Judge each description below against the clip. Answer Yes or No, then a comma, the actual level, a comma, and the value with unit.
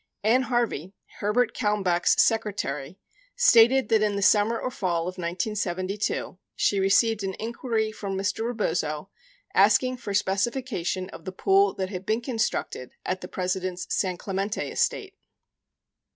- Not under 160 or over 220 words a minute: No, slow, 135 wpm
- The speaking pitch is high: Yes, high, 205 Hz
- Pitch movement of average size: Yes, average, 3.6 semitones